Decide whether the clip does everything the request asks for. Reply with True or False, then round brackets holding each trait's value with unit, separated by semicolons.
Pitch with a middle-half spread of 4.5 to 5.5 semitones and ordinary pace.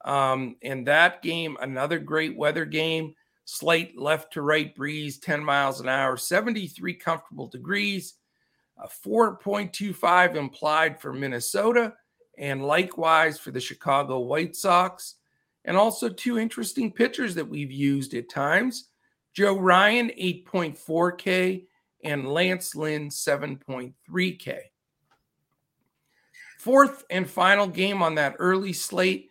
False (4.8 semitones; 120 wpm)